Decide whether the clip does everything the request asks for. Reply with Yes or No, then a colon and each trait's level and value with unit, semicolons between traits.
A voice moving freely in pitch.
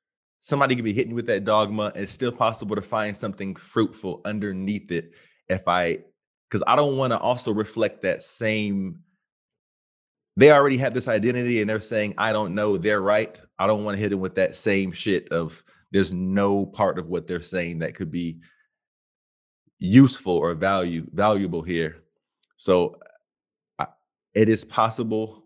No: average, 3.3 semitones